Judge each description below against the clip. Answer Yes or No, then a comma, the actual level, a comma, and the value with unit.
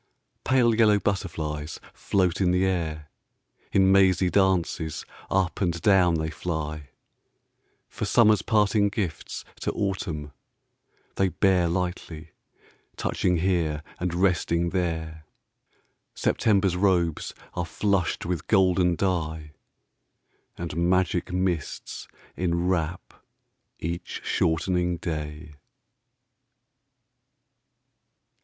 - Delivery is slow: Yes, slow, 80 wpm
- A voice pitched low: Yes, very low, 90 Hz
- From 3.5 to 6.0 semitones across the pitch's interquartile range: No, average, 2.8 semitones